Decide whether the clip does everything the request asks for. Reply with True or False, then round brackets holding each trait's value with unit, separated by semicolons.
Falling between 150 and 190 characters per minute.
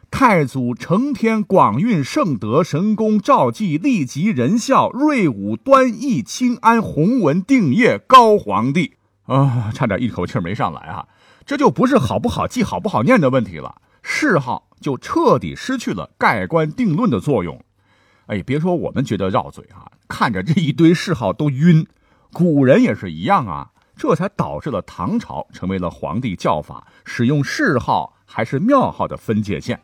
False (245 characters per minute)